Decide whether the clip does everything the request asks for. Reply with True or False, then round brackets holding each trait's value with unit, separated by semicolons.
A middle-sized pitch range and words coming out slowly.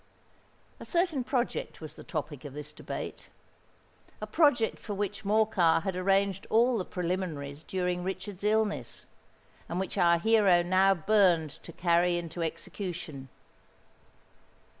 True (3.6 semitones; 125 wpm)